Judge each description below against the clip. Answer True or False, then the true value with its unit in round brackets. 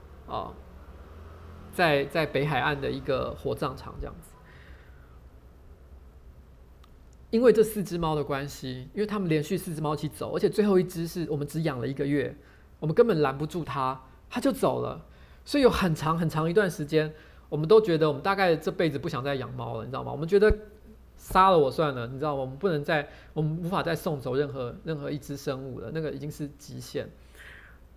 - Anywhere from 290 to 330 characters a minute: True (295 characters per minute)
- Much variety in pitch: True (6.6 semitones)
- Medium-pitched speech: True (150 Hz)